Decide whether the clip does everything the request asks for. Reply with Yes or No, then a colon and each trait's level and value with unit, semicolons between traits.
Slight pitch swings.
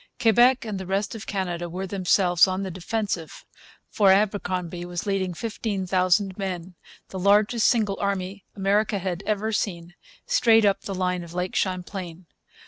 Yes: narrow, 2.3 semitones